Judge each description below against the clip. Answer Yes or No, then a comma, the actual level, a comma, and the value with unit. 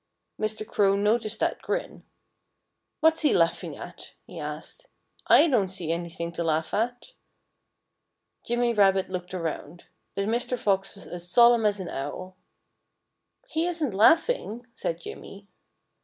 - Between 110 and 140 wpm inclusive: Yes, slow, 135 wpm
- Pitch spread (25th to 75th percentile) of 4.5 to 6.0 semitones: Yes, average, 5.1 semitones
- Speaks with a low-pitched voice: No, high, 200 Hz